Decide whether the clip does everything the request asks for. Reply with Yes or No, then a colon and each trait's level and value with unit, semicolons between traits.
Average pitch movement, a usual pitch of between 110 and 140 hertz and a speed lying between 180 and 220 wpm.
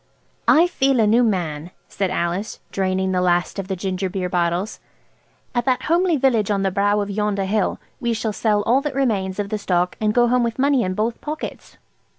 No: average, 4.2 semitones; high, 205 Hz; fast, 205 wpm